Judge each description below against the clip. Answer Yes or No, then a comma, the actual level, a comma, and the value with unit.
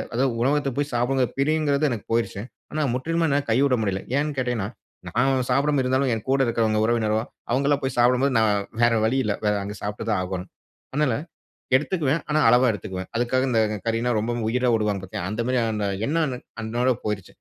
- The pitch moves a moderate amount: Yes, average, 3.8 semitones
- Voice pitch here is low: Yes, low, 125 Hz